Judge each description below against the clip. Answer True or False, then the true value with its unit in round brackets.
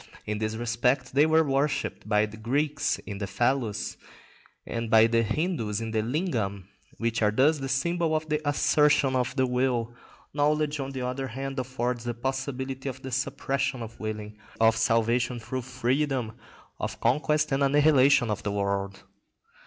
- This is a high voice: False (125 Hz)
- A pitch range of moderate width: True (3.5 semitones)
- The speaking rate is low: False (165 wpm)